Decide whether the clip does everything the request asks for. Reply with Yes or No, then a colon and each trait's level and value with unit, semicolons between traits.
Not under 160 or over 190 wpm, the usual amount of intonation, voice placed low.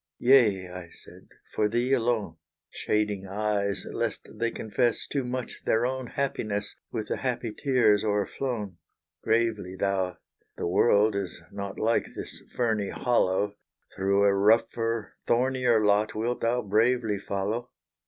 No: slow, 135 wpm; average, 3.1 semitones; low, 110 Hz